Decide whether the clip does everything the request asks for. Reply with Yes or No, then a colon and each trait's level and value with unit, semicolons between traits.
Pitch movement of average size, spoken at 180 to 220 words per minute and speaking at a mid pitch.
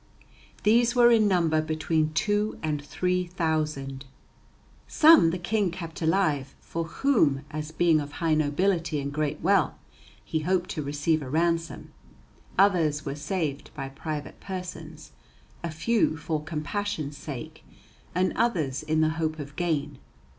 No: average, 3.4 semitones; average, 140 wpm; medium, 160 Hz